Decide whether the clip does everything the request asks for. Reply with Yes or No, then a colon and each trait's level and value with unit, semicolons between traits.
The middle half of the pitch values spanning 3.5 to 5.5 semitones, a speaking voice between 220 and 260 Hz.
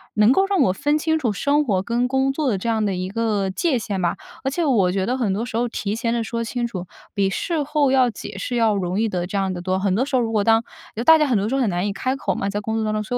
Yes: average, 4.8 semitones; high, 225 Hz